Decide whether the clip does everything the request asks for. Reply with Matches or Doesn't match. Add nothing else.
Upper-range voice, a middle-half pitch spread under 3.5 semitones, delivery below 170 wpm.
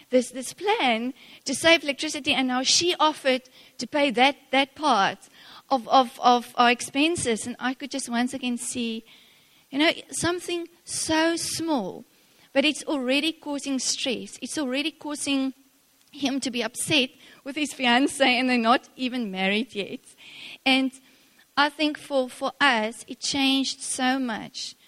Matches